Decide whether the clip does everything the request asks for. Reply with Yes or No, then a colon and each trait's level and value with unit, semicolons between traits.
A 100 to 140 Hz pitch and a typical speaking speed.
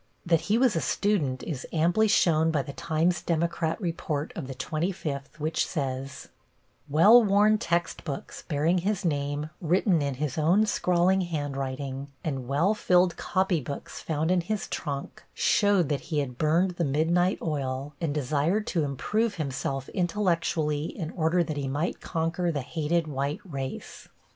No: medium, 160 Hz; average, 160 wpm